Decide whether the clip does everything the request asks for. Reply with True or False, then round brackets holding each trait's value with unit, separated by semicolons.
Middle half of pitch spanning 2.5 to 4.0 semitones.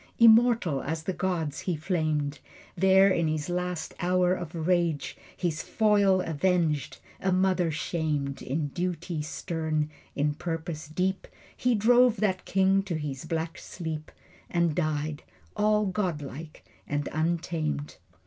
True (3.4 semitones)